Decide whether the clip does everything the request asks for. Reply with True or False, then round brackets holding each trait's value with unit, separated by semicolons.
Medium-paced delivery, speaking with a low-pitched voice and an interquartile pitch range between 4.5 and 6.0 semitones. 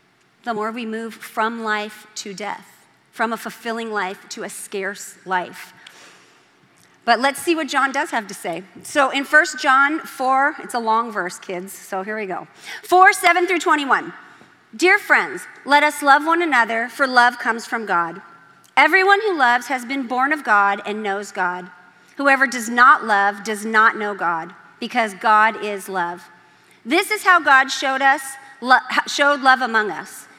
False (175 wpm; 235 Hz; 5.3 semitones)